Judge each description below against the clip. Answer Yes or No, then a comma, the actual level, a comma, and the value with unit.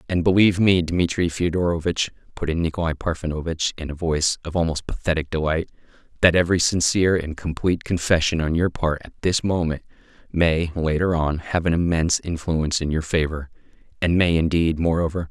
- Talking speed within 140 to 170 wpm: Yes, average, 165 wpm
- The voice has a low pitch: Yes, very low, 85 Hz